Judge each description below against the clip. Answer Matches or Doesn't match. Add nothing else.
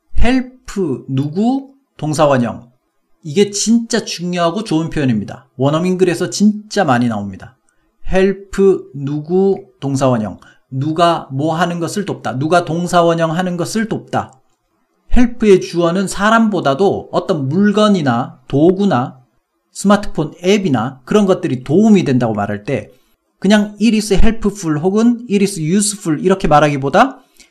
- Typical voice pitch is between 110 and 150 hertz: Doesn't match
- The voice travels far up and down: Matches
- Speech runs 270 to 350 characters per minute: Matches